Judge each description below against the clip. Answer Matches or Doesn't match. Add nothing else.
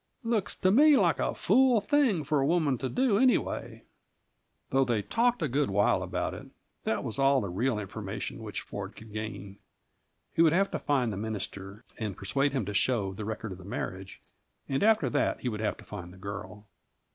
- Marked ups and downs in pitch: Matches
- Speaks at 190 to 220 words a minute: Matches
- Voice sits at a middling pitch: Doesn't match